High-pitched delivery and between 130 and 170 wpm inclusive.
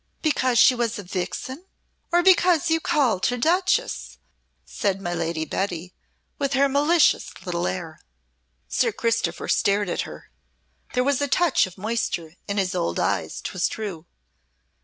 Yes: high, 230 Hz; average, 150 wpm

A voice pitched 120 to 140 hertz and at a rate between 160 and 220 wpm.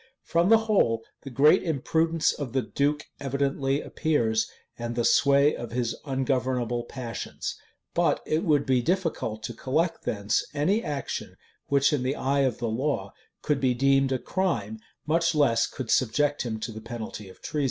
Yes: low, 135 Hz; average, 170 wpm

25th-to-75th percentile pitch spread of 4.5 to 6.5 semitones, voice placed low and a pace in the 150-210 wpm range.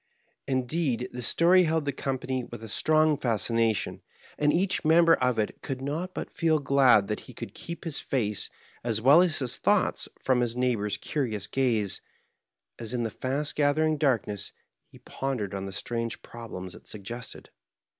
Yes: average, 4.9 semitones; low, 130 Hz; average, 170 wpm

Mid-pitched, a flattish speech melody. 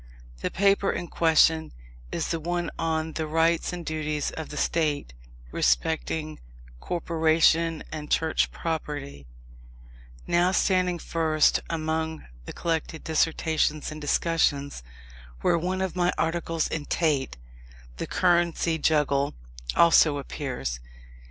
Yes: medium, 160 Hz; narrow, 1.8 semitones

